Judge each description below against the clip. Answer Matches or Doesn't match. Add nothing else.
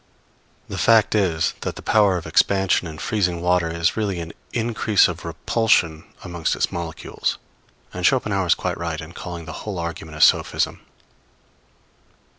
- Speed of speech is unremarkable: Matches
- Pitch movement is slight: Doesn't match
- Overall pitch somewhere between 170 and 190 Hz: Doesn't match